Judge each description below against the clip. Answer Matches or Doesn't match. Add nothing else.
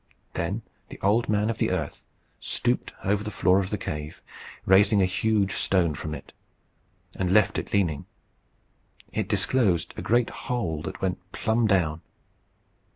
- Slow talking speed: Doesn't match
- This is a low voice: Matches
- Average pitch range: Matches